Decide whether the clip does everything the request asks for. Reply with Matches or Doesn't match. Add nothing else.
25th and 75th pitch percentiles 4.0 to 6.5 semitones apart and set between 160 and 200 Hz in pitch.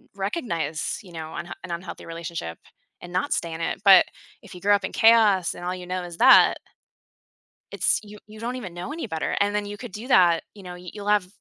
Doesn't match